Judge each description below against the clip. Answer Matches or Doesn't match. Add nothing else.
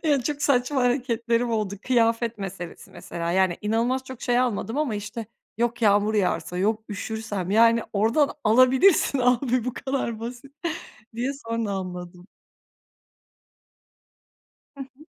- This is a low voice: Doesn't match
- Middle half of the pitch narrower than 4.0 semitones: Matches